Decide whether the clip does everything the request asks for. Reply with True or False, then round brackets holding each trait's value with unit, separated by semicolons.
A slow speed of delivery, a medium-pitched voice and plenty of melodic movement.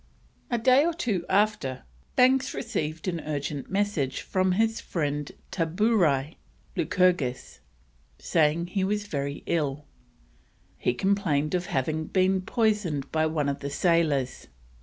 True (125 wpm; 170 Hz; 5.8 semitones)